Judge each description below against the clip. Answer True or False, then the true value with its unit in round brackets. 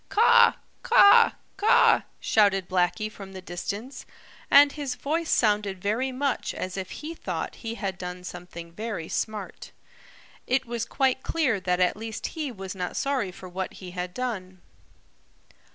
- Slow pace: False (150 wpm)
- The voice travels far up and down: True (6.1 semitones)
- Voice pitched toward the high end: True (210 Hz)